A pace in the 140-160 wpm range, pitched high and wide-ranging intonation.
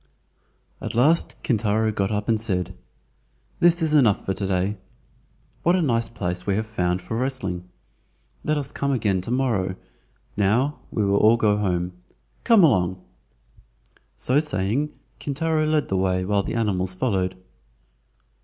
No: average, 150 wpm; low, 110 Hz; wide, 5.9 semitones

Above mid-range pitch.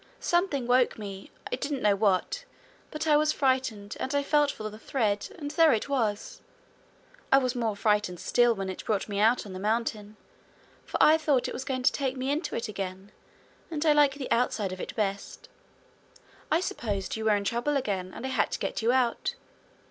Yes: high, 240 Hz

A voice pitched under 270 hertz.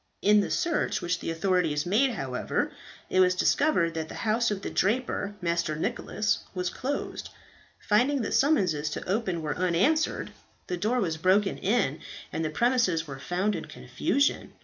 Yes: medium, 185 Hz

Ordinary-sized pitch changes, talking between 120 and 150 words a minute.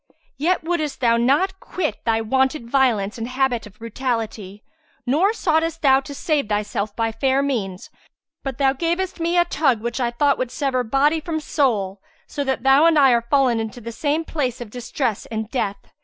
No: average, 4.6 semitones; average, 185 wpm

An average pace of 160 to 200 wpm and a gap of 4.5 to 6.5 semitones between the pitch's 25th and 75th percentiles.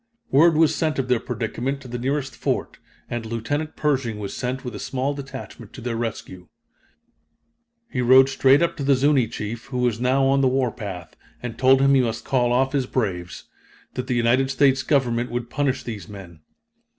No: average, 190 wpm; average, 2.7 semitones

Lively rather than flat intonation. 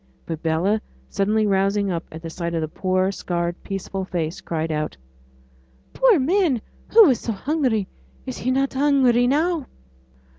Yes: wide, 7.5 semitones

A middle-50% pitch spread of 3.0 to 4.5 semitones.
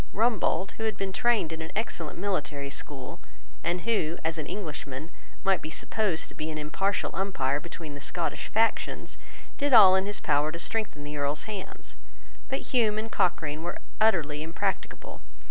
No: average, 5.2 semitones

